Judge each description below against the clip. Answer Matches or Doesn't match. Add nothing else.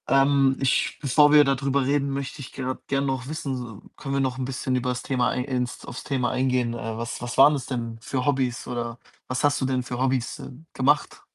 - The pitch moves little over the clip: Matches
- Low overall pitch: Matches